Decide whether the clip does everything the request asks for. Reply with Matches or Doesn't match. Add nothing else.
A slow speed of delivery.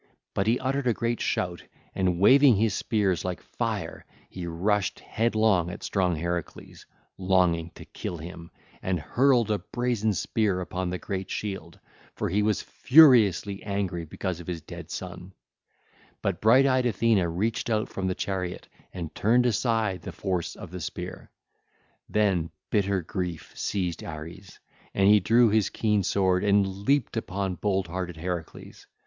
Doesn't match